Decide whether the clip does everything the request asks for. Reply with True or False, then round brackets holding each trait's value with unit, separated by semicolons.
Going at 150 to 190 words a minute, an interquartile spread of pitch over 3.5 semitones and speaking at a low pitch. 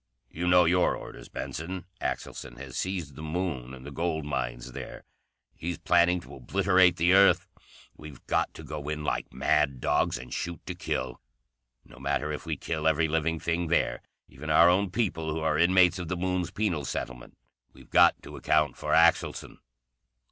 False (175 wpm; 3.2 semitones; 80 Hz)